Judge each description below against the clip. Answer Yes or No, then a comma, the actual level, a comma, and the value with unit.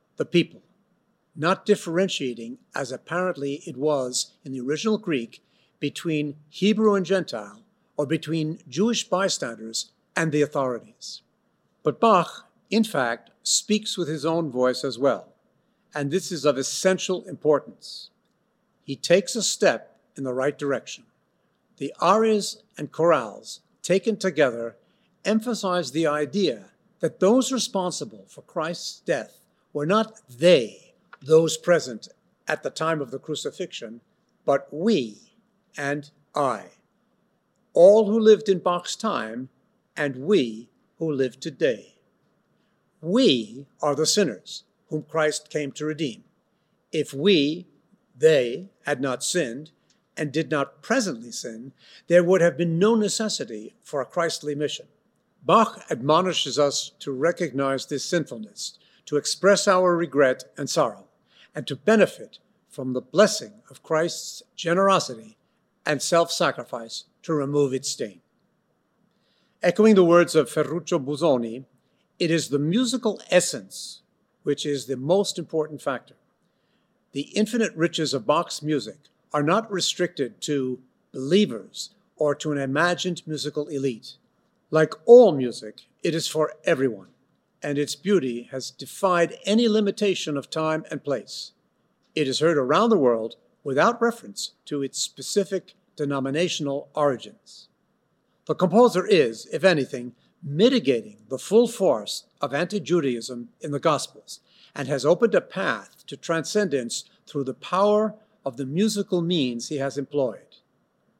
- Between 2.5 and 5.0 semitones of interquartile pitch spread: No, wide, 5.6 semitones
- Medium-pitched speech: Yes, medium, 160 Hz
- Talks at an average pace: No, slow, 130 wpm